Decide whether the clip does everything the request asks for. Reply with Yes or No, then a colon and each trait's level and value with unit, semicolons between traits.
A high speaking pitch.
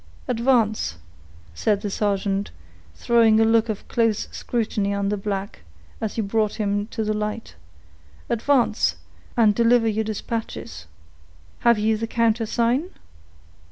Yes: high, 220 Hz